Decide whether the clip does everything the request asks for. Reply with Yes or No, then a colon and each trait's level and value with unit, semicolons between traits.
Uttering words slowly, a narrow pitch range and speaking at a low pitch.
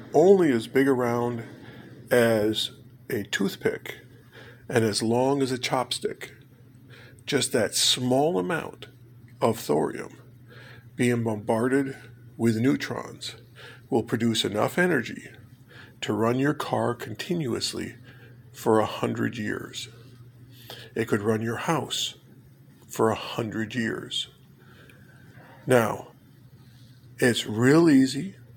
Yes: slow, 105 wpm; narrow, 1.5 semitones; low, 125 Hz